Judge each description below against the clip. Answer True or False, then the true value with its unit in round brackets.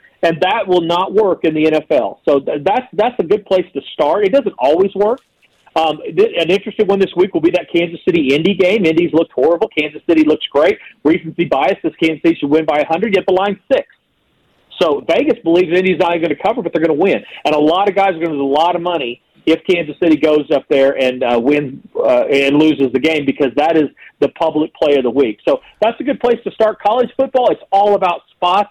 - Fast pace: True (245 wpm)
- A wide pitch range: False (4.0 semitones)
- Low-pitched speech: False (170 Hz)